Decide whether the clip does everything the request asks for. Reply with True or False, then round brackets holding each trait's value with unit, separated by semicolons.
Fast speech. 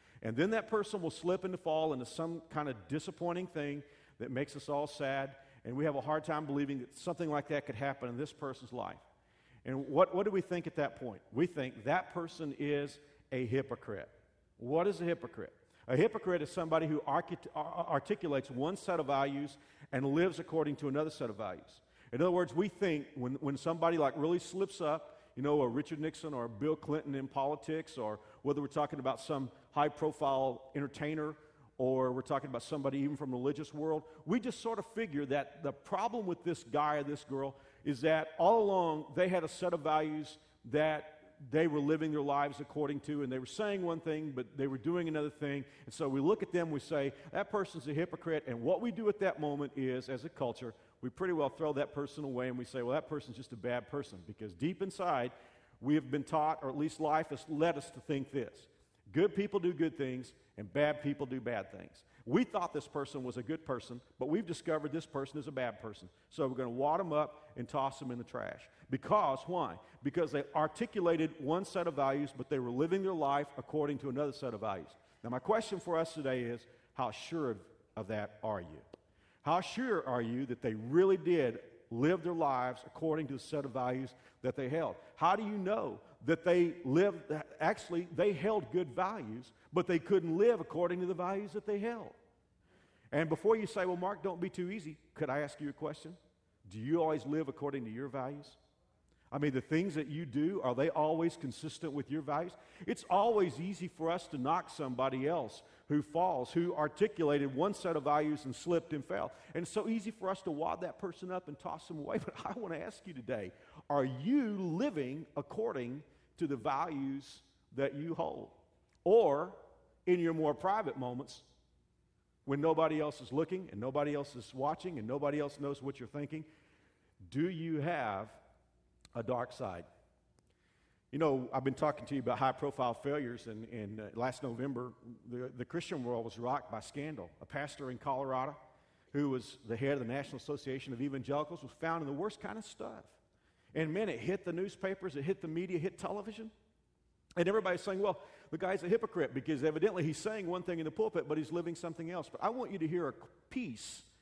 True (210 wpm)